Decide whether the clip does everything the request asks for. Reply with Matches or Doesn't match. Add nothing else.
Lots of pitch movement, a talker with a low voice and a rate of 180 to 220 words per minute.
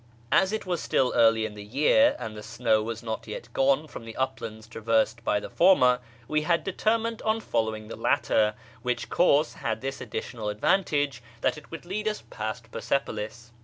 Matches